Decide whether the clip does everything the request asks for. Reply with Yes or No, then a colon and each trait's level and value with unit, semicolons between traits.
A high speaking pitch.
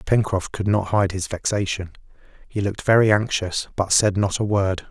No: low, 100 Hz